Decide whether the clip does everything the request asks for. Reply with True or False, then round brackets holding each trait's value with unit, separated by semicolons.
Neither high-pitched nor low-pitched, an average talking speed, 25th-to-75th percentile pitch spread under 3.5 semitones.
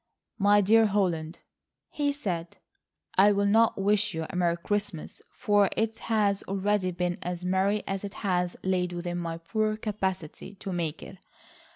False (195 Hz; 160 wpm; 2.8 semitones)